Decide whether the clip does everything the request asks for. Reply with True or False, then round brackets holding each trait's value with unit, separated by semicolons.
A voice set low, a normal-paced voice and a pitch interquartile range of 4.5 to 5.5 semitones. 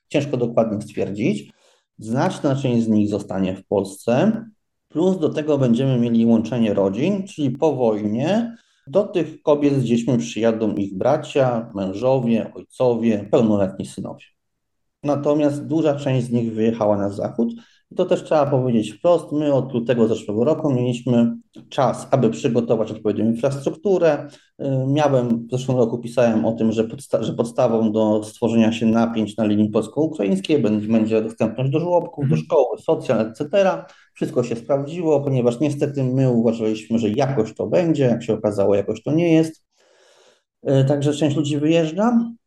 True (125 Hz; 145 wpm; 5.2 semitones)